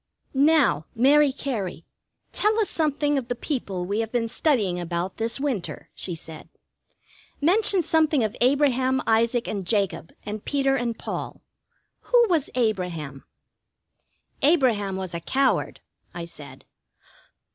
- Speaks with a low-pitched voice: No, high, 235 Hz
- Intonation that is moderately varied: No, wide, 7.1 semitones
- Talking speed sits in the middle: No, slow, 130 wpm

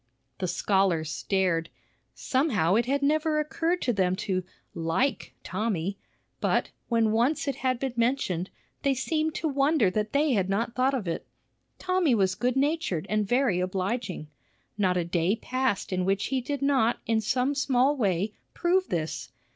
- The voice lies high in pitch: Yes, high, 230 Hz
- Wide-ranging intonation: Yes, wide, 6.7 semitones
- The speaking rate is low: No, average, 165 wpm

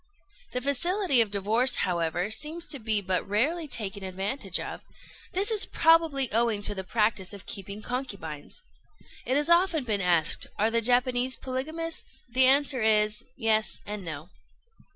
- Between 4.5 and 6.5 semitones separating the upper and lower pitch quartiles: Yes, wide, 5.5 semitones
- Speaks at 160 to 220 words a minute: No, average, 150 wpm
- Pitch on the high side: Yes, high, 230 Hz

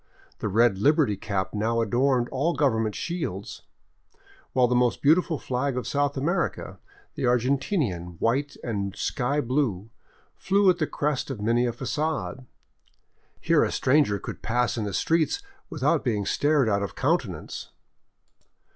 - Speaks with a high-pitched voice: No, low, 125 Hz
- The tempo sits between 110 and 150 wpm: Yes, average, 145 wpm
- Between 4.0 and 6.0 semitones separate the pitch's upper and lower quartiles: Yes, average, 4.9 semitones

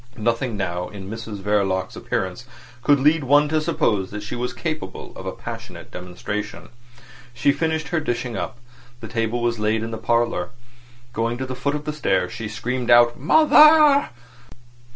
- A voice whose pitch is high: No, low, 120 Hz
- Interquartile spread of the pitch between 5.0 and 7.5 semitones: Yes, wide, 5.6 semitones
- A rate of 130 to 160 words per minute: No, average, 170 wpm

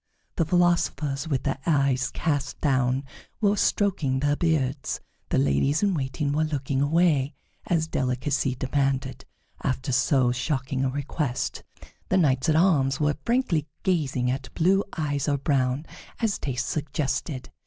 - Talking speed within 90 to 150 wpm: Yes, average, 140 wpm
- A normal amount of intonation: Yes, average, 3.3 semitones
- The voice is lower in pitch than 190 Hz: Yes, medium, 140 Hz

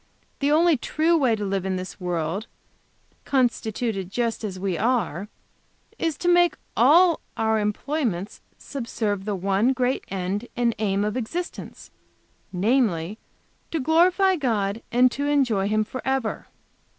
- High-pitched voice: Yes, high, 225 Hz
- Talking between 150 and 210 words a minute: No, slow, 135 wpm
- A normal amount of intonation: No, wide, 5.8 semitones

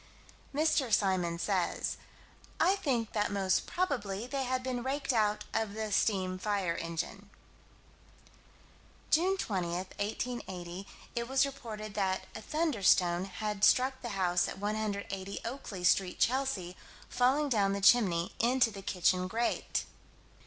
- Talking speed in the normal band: No, slow, 130 wpm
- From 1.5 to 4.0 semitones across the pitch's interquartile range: No, average, 5.0 semitones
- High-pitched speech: Yes, high, 210 Hz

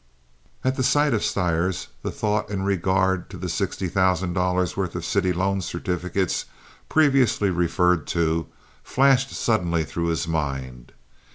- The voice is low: Yes, very low, 90 Hz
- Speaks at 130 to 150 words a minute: Yes, average, 145 wpm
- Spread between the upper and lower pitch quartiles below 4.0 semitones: Yes, average, 2.8 semitones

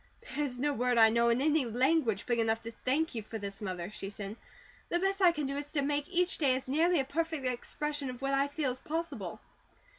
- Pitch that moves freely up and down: No, average, 4.5 semitones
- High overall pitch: Yes, very high, 270 Hz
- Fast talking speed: Yes, fast, 230 wpm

